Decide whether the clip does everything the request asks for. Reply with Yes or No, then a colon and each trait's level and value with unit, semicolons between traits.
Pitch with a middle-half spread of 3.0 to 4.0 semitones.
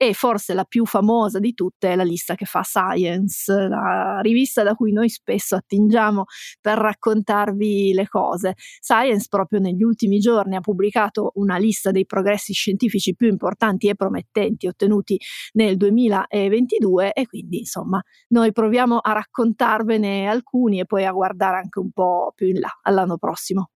No: narrow, 2.4 semitones